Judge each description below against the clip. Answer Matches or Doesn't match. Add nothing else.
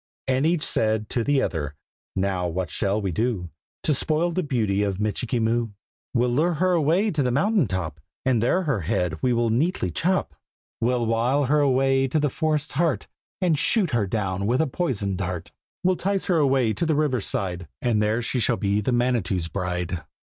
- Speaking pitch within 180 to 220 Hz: Doesn't match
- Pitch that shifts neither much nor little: Doesn't match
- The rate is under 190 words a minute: Doesn't match